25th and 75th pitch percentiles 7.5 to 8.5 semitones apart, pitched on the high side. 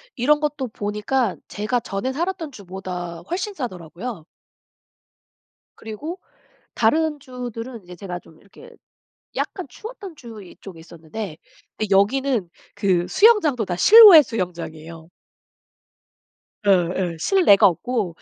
Yes: wide, 8.1 semitones; high, 220 Hz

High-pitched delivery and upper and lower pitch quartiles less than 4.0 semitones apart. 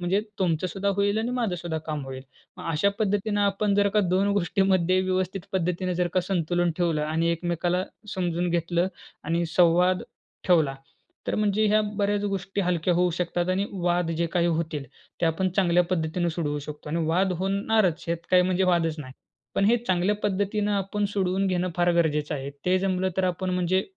No: medium, 180 Hz; narrow, 2.4 semitones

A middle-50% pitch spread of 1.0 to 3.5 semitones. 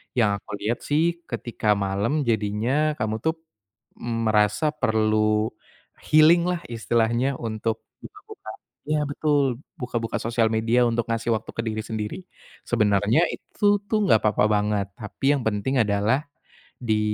No: average, 4.3 semitones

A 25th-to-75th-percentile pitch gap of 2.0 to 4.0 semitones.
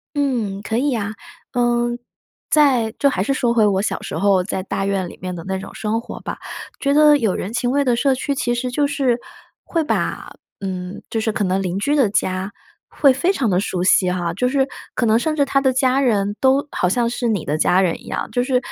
No: wide, 5.4 semitones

